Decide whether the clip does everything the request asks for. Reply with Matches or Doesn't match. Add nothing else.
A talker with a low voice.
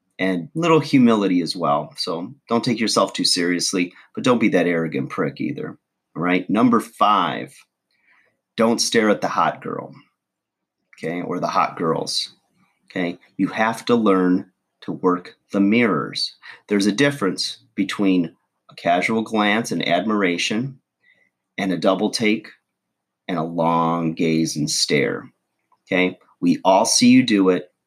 Matches